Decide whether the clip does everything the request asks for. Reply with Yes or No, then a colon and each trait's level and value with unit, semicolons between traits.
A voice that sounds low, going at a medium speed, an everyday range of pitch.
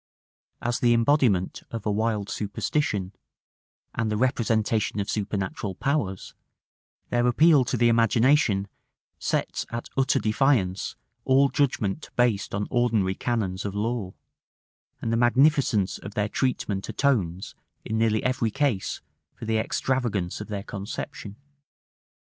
No: low, 110 Hz; slow, 125 wpm; average, 3.6 semitones